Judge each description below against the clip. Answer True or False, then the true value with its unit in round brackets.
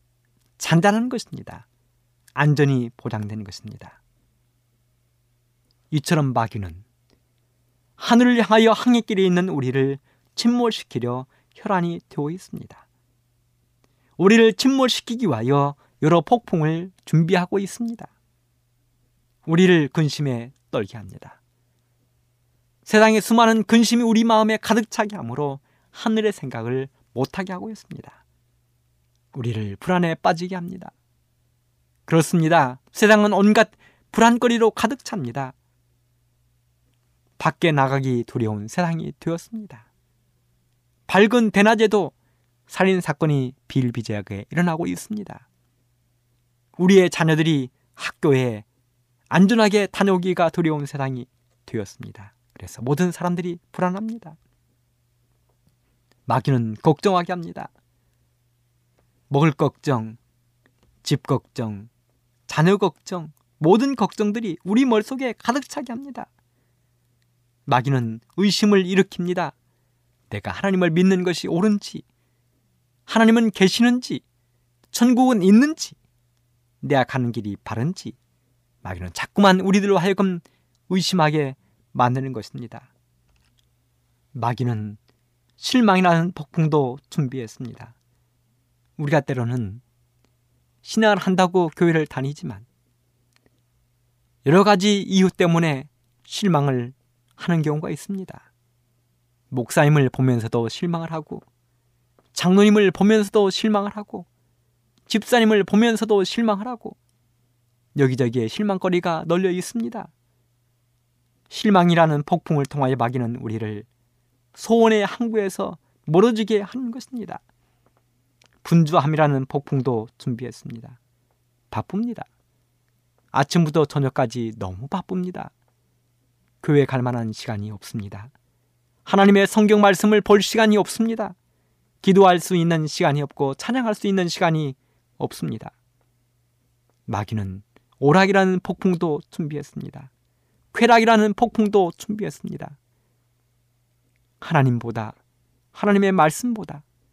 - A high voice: False (135 Hz)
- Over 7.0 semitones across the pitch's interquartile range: True (7.6 semitones)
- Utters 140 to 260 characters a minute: True (255 characters per minute)